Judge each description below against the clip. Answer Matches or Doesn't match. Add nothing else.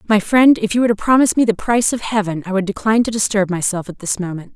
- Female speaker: Matches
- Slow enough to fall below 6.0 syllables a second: Doesn't match